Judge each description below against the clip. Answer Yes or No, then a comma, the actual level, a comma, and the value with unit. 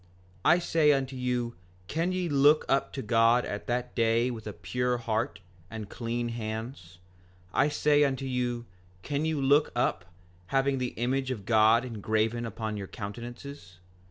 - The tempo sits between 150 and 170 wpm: Yes, average, 160 wpm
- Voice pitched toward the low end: Yes, low, 120 Hz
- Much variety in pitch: No, average, 3.4 semitones